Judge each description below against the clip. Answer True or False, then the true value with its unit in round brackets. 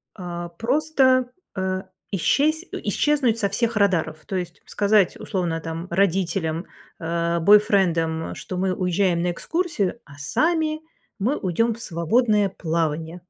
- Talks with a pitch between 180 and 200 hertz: True (190 Hz)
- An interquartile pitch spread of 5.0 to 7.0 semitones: True (5.3 semitones)